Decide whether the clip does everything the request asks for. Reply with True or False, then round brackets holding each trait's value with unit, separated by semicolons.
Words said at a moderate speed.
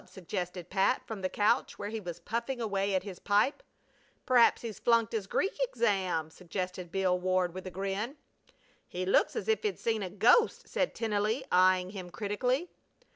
True (175 wpm)